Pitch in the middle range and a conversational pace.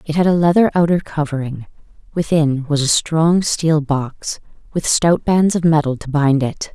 Yes: medium, 155 Hz; average, 180 wpm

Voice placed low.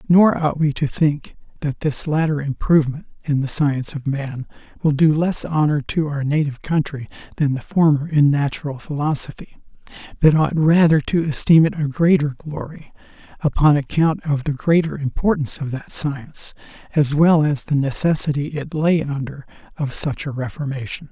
No: medium, 150 Hz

